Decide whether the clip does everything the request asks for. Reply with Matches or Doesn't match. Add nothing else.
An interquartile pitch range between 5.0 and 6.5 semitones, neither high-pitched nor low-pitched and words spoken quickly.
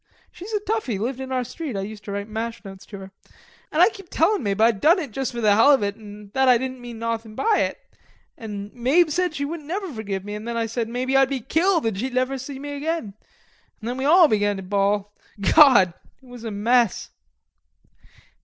Doesn't match